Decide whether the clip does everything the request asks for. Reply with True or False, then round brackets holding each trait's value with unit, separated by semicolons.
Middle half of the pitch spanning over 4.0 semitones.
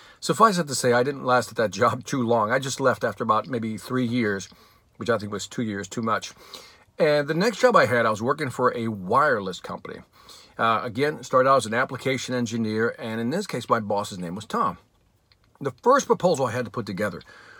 False (2.9 semitones)